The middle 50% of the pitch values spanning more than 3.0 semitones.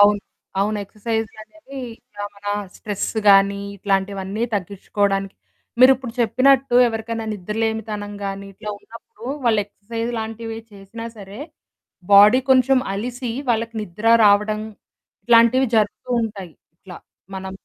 No: narrow, 2.6 semitones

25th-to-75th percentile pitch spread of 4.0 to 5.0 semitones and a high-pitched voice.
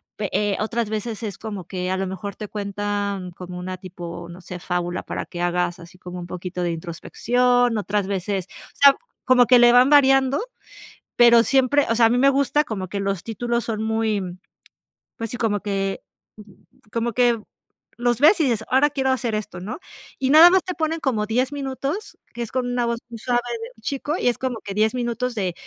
Yes: average, 4.4 semitones; high, 225 Hz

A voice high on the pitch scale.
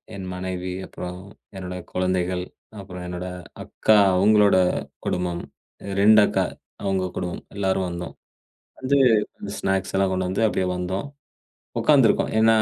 No: very low, 95 Hz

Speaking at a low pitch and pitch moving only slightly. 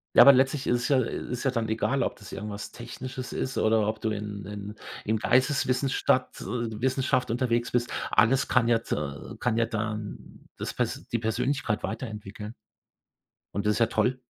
No: low, 115 Hz; average, 3.2 semitones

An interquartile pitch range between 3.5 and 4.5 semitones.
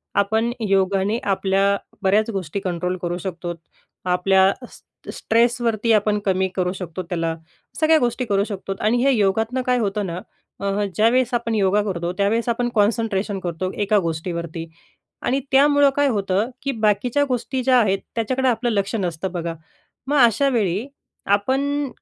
Yes: average, 4.0 semitones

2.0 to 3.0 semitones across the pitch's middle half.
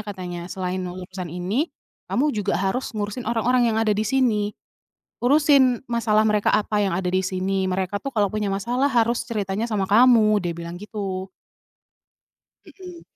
No: average, 3.9 semitones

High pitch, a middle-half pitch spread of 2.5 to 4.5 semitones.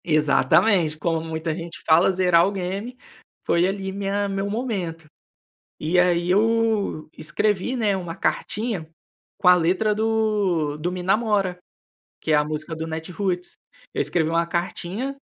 No: medium, 180 Hz; average, 3.8 semitones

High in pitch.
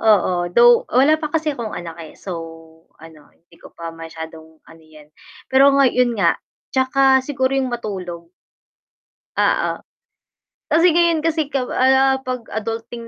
Yes: high, 235 Hz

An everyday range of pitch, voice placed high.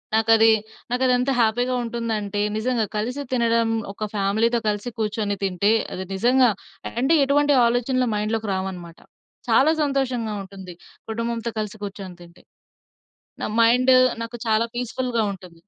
Yes: average, 3.2 semitones; high, 225 Hz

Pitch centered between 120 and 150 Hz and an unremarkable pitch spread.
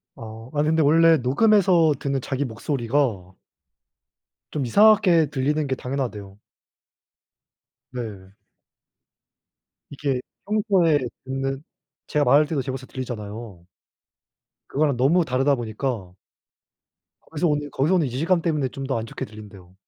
Yes: low, 135 Hz; average, 4.6 semitones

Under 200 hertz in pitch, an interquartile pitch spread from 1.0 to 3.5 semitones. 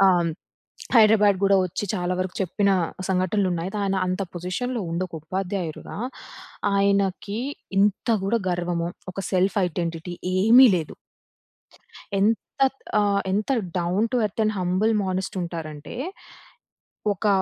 Yes: high, 190 Hz; narrow, 2.5 semitones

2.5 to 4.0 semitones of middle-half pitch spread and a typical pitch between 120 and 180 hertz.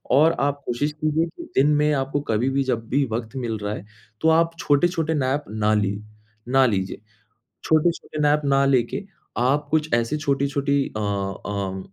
No: average, 4.7 semitones; medium, 140 Hz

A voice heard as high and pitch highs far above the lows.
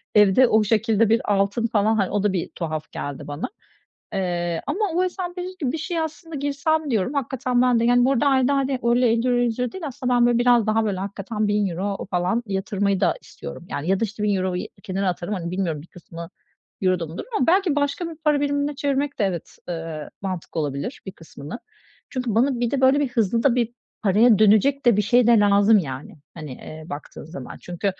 Yes: high, 220 Hz; wide, 5.8 semitones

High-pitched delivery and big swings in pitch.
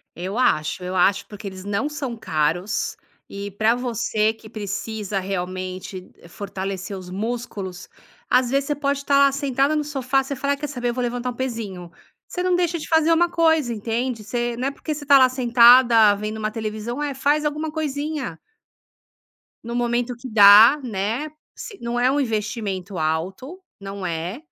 Yes: high, 235 Hz; wide, 5.7 semitones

